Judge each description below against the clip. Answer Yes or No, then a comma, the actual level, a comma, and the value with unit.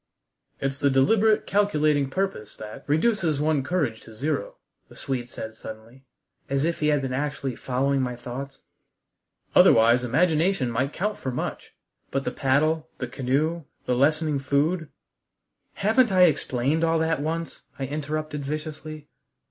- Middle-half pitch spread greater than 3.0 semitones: Yes, average, 3.5 semitones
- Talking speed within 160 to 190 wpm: No, average, 150 wpm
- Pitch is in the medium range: Yes, medium, 145 Hz